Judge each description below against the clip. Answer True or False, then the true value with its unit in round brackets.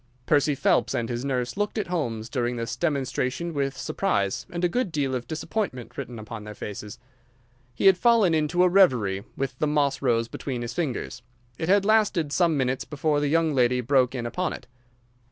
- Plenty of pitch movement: True (5.9 semitones)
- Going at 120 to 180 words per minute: False (190 wpm)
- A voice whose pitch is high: False (140 Hz)